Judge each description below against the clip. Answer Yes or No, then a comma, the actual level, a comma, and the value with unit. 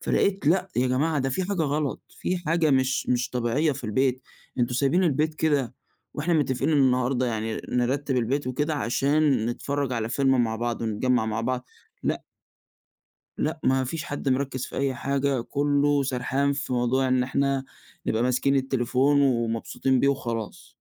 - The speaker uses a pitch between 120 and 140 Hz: Yes, low, 135 Hz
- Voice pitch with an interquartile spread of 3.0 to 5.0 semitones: No, narrow, 2.5 semitones